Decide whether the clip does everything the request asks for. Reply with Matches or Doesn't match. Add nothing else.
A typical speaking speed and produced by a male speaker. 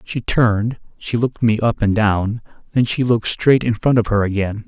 Doesn't match